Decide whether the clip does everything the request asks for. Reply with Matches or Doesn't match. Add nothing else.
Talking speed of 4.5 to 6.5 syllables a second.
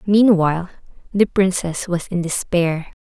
Doesn't match